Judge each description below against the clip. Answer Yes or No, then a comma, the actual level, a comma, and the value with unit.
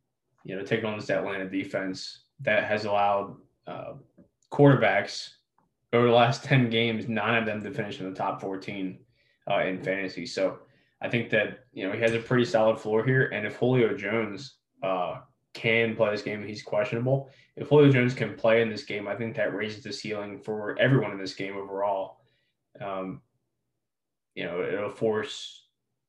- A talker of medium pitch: No, low, 110 Hz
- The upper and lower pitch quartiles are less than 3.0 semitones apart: Yes, narrow, 2.6 semitones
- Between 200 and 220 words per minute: No, average, 180 wpm